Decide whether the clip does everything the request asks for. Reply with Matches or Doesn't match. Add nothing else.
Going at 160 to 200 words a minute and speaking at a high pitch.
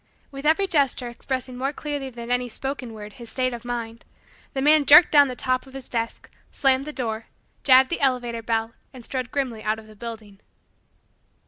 Matches